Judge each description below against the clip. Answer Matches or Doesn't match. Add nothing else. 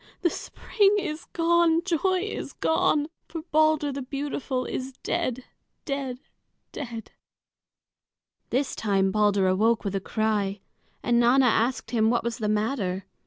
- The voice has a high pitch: Matches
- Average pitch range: Doesn't match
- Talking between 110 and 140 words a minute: Matches